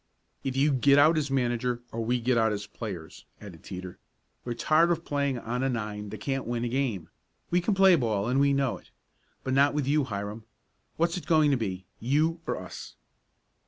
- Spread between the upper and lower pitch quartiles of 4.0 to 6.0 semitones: Yes, average, 4.5 semitones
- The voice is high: No, low, 125 Hz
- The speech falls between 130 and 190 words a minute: No, fast, 205 wpm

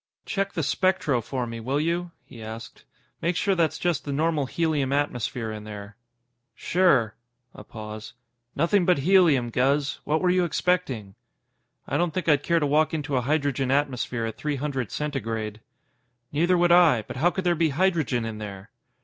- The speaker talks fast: No, average, 175 wpm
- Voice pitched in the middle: Yes, medium, 145 Hz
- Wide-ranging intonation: Yes, wide, 6.1 semitones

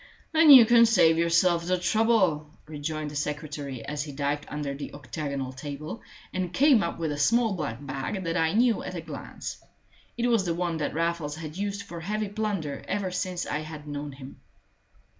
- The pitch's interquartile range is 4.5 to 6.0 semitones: Yes, average, 4.9 semitones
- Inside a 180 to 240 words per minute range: Yes, average, 190 wpm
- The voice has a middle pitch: Yes, medium, 165 Hz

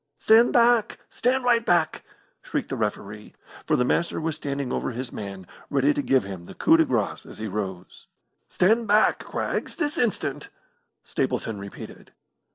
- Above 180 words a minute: No, average, 165 wpm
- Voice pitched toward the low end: No, medium, 145 Hz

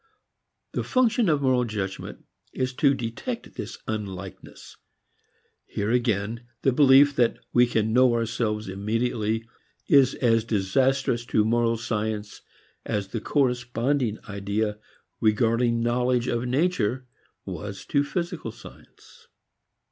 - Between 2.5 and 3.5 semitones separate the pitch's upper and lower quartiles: Yes, average, 3.2 semitones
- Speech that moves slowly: Yes, slow, 115 wpm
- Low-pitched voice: Yes, low, 115 Hz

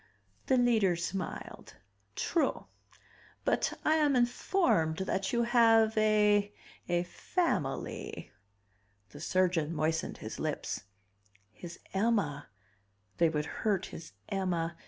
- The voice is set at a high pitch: Yes, high, 195 Hz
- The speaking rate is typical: No, slow, 105 wpm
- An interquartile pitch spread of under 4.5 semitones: No, wide, 5.6 semitones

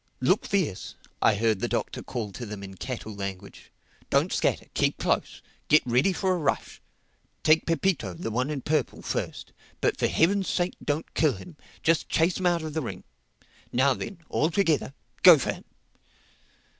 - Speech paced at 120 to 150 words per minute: No, average, 170 wpm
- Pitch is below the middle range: No, medium, 145 Hz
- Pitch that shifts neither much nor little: No, wide, 6.8 semitones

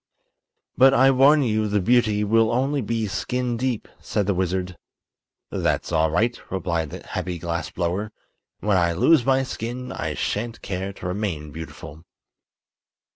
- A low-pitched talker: Yes, low, 105 Hz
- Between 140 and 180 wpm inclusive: Yes, average, 150 wpm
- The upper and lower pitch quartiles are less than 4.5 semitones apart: No, average, 5.3 semitones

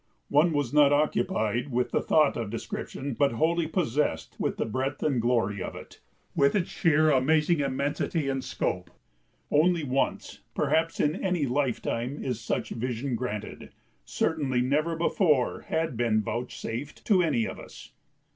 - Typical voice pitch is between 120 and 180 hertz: Yes, medium, 140 Hz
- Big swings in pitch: No, average, 4.3 semitones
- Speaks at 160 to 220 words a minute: No, average, 150 wpm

